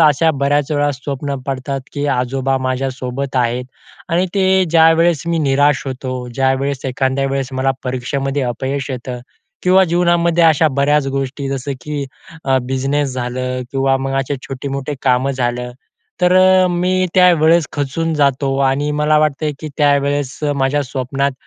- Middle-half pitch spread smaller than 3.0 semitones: Yes, narrow, 2.4 semitones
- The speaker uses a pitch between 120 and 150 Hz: Yes, medium, 140 Hz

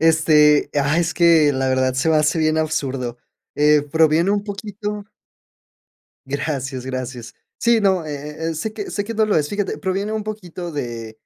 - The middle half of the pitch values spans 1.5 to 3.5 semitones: No, wide, 5.5 semitones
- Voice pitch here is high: No, medium, 155 Hz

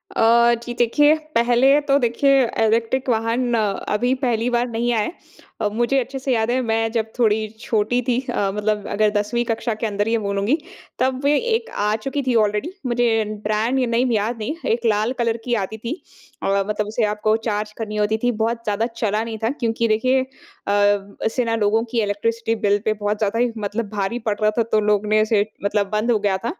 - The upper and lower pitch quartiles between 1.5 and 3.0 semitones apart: Yes, narrow, 2.4 semitones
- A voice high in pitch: Yes, high, 225 Hz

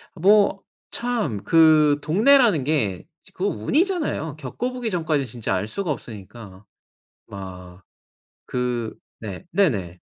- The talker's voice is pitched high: No, medium, 145 Hz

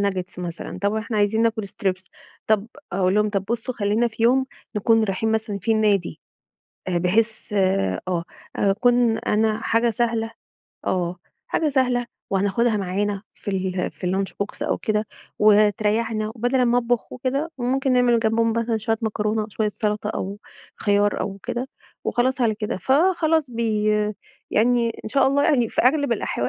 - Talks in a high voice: Yes, high, 220 Hz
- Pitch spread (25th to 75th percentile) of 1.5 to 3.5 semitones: Yes, average, 2.9 semitones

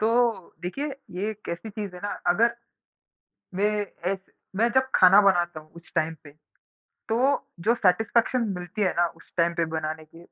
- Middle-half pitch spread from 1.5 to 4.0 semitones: No, average, 4.4 semitones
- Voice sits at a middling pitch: No, high, 195 Hz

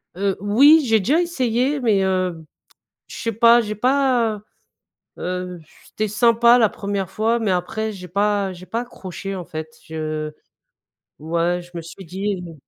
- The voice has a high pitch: Yes, high, 200 Hz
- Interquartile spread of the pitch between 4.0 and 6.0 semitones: Yes, average, 4.4 semitones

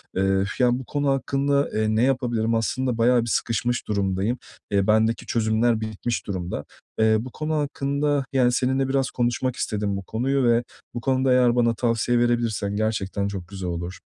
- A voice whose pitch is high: No, low, 120 Hz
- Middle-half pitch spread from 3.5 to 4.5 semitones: No, average, 3.1 semitones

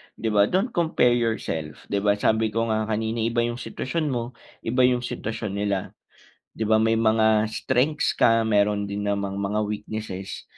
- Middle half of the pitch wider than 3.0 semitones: No, narrow, 2.4 semitones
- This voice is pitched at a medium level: No, low, 110 Hz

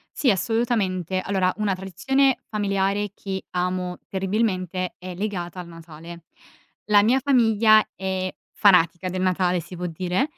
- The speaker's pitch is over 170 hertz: Yes, high, 190 Hz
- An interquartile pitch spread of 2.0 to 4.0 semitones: Yes, average, 2.7 semitones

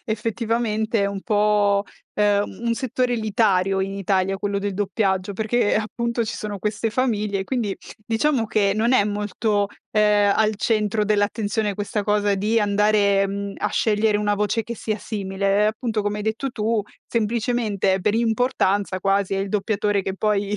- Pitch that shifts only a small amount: Yes, narrow, 1.7 semitones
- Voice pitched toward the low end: No, high, 210 Hz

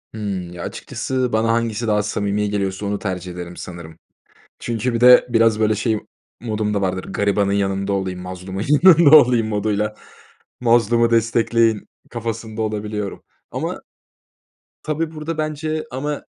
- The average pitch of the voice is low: Yes, low, 110 Hz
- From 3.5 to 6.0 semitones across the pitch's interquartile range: No, average, 2.9 semitones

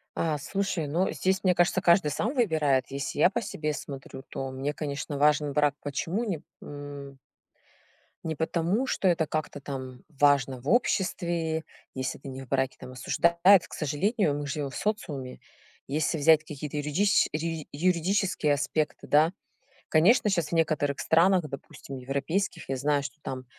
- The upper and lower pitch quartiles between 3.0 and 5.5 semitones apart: Yes, average, 3.7 semitones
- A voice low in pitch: No, medium, 150 Hz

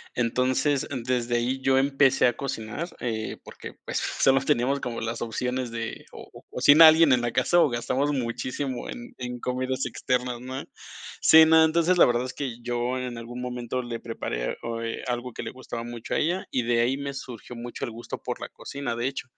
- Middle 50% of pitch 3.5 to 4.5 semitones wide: No, narrow, 2.4 semitones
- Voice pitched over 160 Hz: No, low, 125 Hz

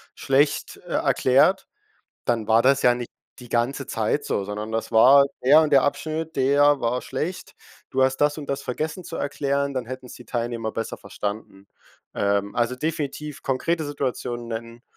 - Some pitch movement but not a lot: Yes, average, 3.6 semitones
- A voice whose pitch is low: Yes, low, 130 Hz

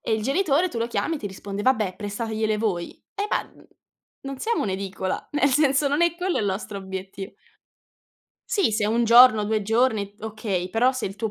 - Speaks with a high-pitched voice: Yes, high, 220 Hz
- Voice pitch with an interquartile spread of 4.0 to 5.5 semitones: Yes, average, 4.8 semitones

